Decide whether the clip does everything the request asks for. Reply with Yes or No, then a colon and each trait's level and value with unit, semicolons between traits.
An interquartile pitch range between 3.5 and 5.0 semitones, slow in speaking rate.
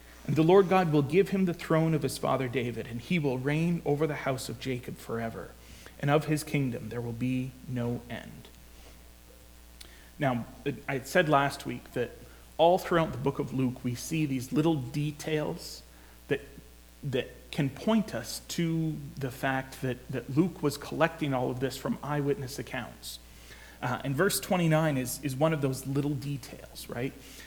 No: average, 4.3 semitones; average, 175 wpm